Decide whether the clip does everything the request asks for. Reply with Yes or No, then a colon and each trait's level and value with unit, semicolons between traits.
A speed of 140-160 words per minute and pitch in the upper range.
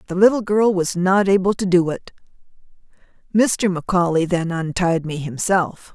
No: average, 150 wpm; medium, 180 Hz